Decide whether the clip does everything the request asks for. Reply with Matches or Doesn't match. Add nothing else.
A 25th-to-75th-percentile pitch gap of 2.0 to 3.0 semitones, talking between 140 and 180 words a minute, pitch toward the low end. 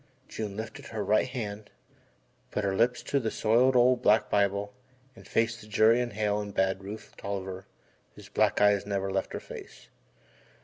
Matches